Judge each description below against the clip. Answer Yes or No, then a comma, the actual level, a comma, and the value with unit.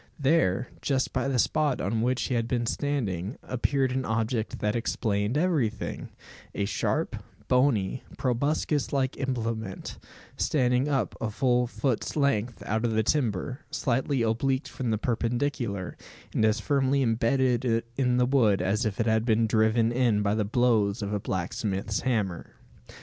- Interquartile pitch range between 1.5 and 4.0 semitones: Yes, average, 3.4 semitones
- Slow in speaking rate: No, average, 155 wpm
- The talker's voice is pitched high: No, low, 120 Hz